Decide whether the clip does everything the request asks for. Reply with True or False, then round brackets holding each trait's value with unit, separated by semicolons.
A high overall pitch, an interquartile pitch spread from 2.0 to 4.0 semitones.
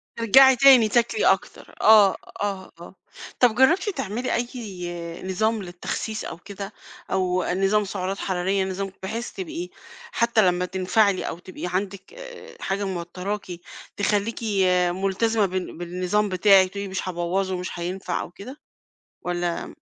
True (195 Hz; 3.3 semitones)